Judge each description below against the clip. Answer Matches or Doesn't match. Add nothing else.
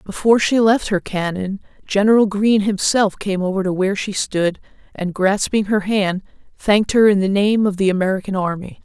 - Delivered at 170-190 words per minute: Matches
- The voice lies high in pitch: Matches